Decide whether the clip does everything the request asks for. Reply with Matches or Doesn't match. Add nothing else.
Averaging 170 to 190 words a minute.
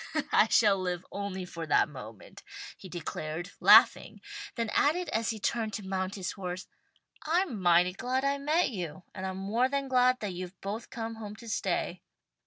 Matches